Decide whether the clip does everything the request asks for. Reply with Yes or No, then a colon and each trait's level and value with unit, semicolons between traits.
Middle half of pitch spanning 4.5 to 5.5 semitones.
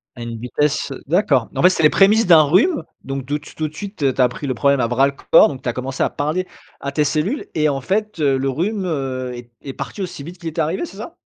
Yes: average, 5.2 semitones